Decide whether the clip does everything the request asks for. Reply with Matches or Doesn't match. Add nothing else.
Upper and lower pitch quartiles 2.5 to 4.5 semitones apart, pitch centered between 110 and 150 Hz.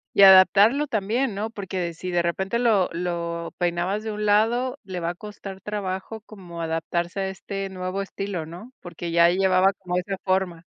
Doesn't match